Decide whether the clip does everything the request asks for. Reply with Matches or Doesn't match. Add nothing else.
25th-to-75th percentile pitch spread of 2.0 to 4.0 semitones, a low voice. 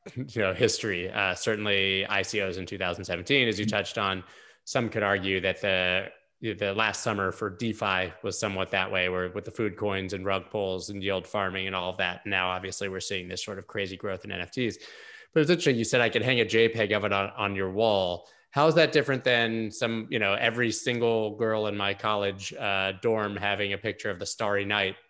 Matches